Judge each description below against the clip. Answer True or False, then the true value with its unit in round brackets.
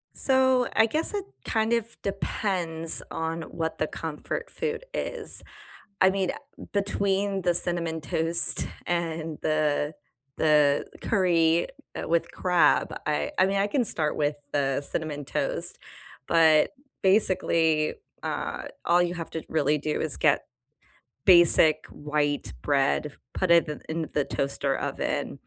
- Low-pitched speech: False (165 Hz)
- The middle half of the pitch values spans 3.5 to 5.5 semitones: True (4.1 semitones)